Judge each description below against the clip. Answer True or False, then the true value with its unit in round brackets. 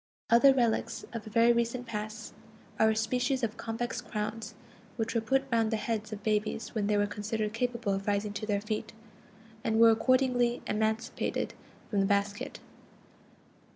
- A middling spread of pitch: False (1.8 semitones)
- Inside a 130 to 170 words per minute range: True (165 wpm)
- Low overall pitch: False (220 Hz)